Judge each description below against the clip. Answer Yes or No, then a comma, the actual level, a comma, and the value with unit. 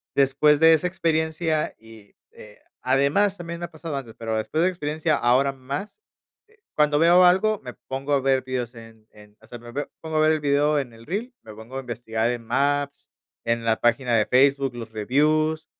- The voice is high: No, medium, 140 Hz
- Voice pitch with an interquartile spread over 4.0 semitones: Yes, average, 4.9 semitones